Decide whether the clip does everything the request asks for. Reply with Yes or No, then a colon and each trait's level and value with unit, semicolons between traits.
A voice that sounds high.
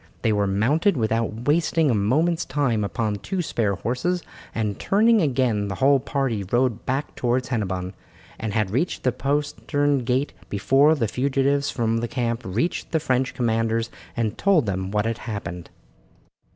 No: low, 120 Hz